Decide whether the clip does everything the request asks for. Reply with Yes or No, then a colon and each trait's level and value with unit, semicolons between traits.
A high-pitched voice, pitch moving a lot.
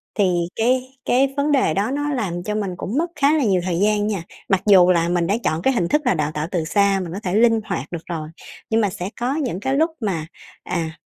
Yes: high, 200 Hz; wide, 6.5 semitones